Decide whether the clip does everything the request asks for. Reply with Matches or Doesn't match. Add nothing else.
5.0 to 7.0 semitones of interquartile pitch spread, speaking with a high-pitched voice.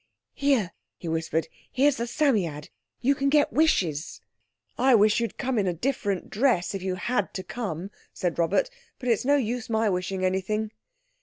Matches